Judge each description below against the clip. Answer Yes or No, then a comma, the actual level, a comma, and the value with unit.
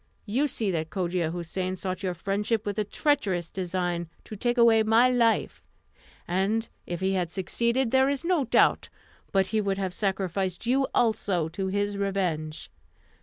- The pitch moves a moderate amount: Yes, average, 3.8 semitones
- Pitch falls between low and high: No, high, 195 Hz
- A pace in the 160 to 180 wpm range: Yes, average, 165 wpm